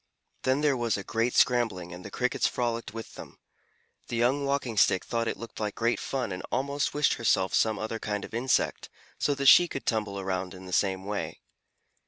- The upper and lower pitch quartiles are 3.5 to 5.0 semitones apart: Yes, average, 4.3 semitones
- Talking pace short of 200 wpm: No, fast, 205 wpm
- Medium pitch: No, low, 115 Hz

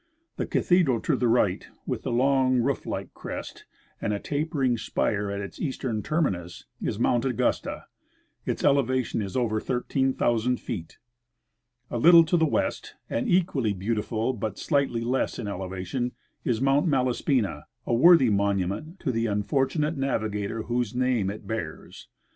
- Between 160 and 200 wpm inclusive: No, average, 150 wpm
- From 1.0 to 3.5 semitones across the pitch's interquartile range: No, average, 4.4 semitones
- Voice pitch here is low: Yes, low, 120 Hz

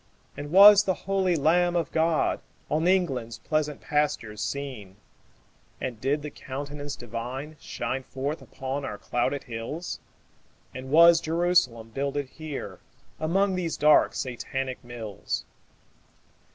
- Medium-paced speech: No, slow, 120 wpm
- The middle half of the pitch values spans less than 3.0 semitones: No, average, 4.2 semitones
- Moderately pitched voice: Yes, medium, 145 Hz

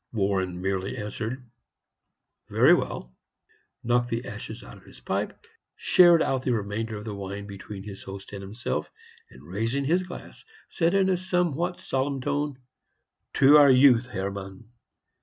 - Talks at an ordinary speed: Yes, average, 150 wpm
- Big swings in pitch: Yes, wide, 6.3 semitones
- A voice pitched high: No, low, 115 Hz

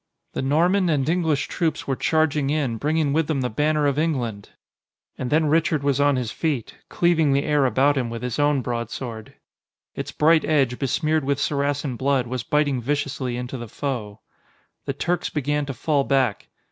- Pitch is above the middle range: No, medium, 140 Hz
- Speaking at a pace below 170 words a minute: No, average, 180 wpm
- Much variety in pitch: No, average, 3.2 semitones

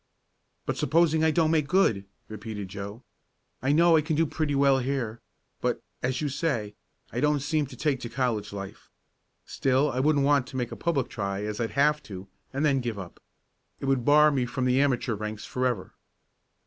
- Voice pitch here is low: Yes, low, 130 Hz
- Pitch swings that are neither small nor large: Yes, average, 4.9 semitones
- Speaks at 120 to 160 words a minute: No, average, 200 wpm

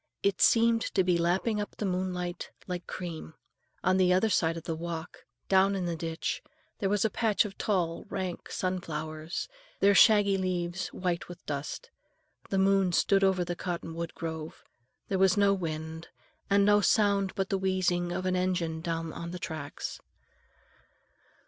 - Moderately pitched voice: Yes, medium, 180 Hz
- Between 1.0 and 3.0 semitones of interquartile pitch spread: Yes, narrow, 2.6 semitones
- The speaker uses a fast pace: No, average, 165 wpm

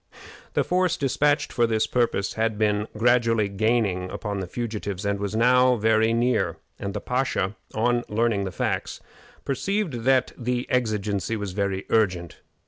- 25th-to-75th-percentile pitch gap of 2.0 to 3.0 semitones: No, average, 3.4 semitones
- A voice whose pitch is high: No, low, 110 Hz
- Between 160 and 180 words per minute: No, average, 150 wpm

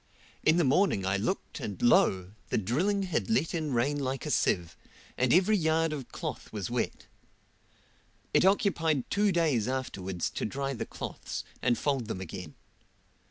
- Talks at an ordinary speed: Yes, average, 160 wpm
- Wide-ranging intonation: Yes, wide, 7.3 semitones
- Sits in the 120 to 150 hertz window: Yes, low, 135 Hz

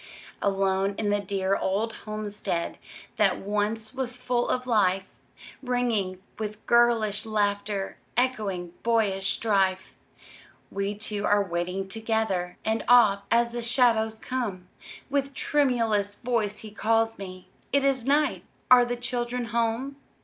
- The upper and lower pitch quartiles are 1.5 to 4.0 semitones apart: Yes, average, 3.3 semitones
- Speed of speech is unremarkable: No, slow, 130 wpm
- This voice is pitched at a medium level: No, high, 220 Hz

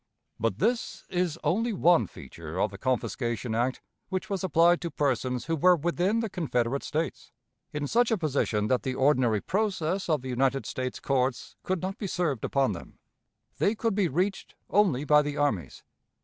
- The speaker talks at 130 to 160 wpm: No, average, 175 wpm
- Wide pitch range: Yes, wide, 6.4 semitones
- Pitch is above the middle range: No, medium, 150 Hz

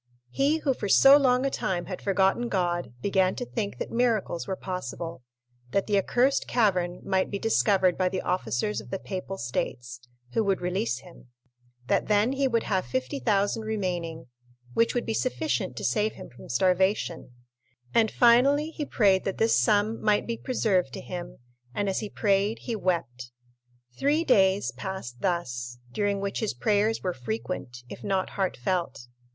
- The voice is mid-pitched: No, high, 195 Hz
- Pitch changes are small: No, average, 4.3 semitones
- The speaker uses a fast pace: No, average, 165 wpm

